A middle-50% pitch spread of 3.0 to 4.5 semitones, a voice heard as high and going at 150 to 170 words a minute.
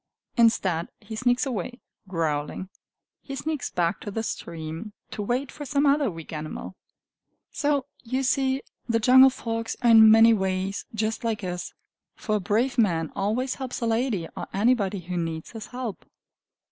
No: average, 5.3 semitones; high, 225 Hz; average, 160 wpm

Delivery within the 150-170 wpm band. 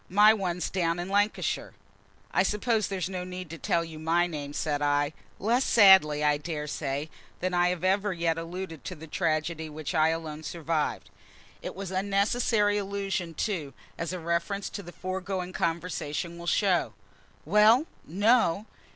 Yes: average, 160 wpm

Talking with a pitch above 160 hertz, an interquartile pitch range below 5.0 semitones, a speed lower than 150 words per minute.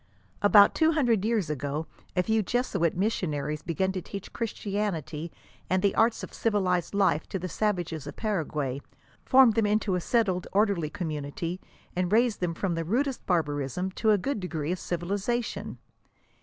No: medium, 185 Hz; average, 4.6 semitones; average, 170 wpm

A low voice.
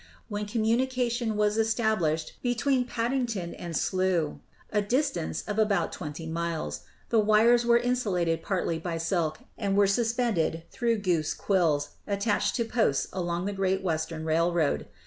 No: high, 200 Hz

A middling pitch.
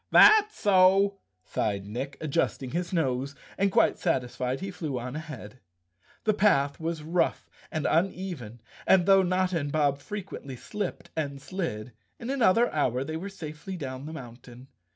Yes: medium, 155 Hz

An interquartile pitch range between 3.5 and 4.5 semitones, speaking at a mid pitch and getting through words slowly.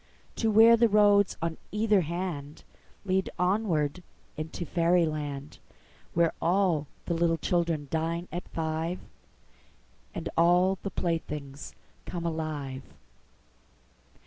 No: average, 3.1 semitones; medium, 170 Hz; slow, 95 wpm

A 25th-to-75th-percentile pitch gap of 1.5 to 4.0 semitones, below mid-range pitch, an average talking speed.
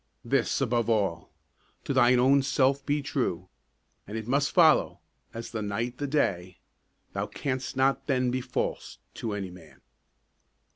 No: average, 4.7 semitones; low, 125 Hz; average, 150 wpm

